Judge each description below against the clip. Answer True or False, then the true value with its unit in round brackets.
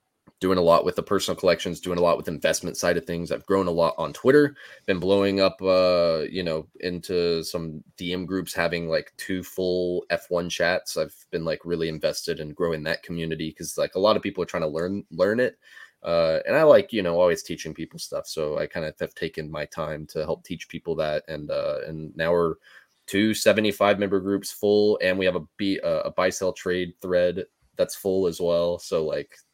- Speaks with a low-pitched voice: True (90 Hz)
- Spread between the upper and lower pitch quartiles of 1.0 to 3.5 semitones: True (2.7 semitones)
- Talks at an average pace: False (215 wpm)